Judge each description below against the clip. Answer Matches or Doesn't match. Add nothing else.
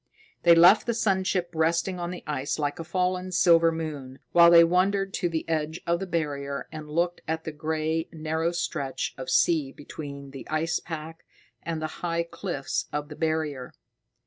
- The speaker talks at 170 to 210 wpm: Matches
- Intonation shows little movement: Matches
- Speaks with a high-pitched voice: Doesn't match